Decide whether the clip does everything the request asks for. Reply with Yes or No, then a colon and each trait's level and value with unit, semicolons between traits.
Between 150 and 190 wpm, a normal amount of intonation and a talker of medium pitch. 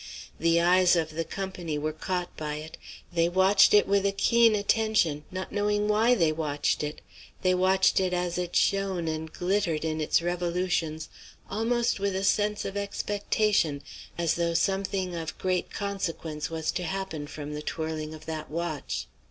Yes: average, 170 wpm; average, 3.7 semitones; medium, 180 Hz